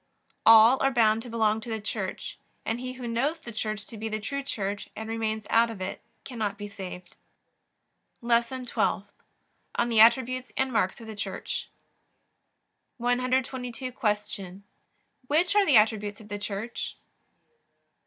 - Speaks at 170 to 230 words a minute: No, average, 155 wpm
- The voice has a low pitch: No, high, 225 Hz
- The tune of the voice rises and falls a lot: No, average, 3.0 semitones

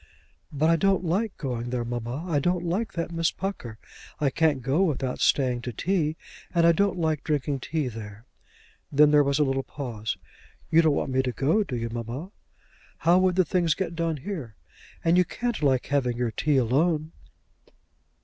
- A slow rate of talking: No, average, 190 wpm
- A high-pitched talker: No, medium, 150 Hz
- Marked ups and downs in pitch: No, average, 5.0 semitones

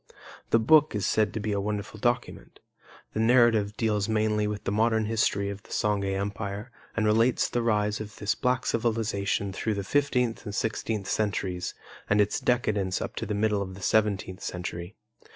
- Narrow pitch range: Yes, narrow, 2.0 semitones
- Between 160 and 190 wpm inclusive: Yes, average, 180 wpm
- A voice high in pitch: No, low, 105 Hz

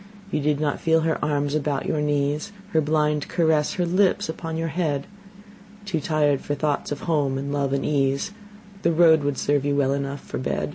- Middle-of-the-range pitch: Yes, medium, 150 Hz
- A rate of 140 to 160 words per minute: No, average, 200 wpm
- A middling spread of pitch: No, narrow, 2.1 semitones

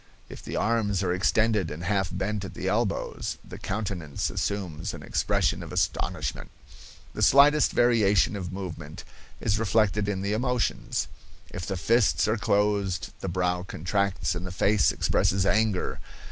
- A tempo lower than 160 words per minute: Yes, average, 150 wpm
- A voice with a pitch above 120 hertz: No, low, 100 Hz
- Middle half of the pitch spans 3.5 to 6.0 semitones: No, average, 2.9 semitones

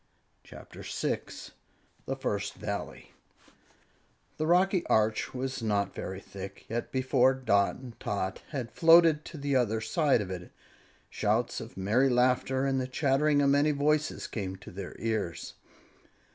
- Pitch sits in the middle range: No, low, 130 Hz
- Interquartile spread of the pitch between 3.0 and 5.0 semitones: No, wide, 5.6 semitones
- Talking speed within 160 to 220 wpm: No, average, 145 wpm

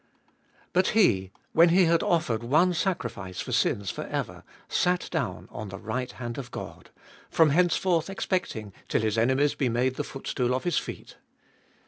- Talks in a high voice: No, low, 130 Hz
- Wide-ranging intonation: Yes, wide, 7.5 semitones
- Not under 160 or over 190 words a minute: Yes, average, 165 wpm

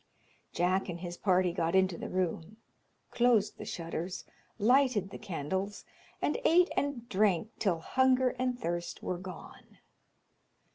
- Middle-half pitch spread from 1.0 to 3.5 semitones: No, wide, 5.6 semitones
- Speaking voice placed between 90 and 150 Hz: No, high, 190 Hz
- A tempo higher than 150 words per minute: No, slow, 135 wpm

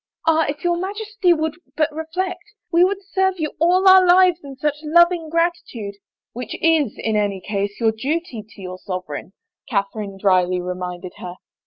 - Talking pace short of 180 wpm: No, average, 185 wpm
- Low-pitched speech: No, very high, 300 Hz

